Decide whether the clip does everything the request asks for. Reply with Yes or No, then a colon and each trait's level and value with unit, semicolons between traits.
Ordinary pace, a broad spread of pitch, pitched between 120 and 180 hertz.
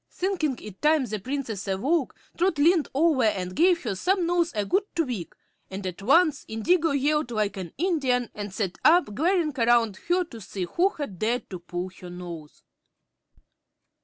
No: average, 165 wpm; wide, 8.9 semitones; very high, 250 Hz